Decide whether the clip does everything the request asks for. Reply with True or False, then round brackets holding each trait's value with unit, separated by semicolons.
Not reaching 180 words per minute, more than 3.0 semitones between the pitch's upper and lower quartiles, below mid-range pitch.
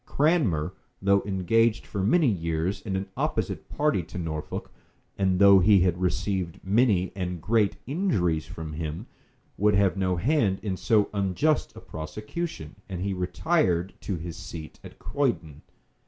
True (150 wpm; 3.7 semitones; 95 Hz)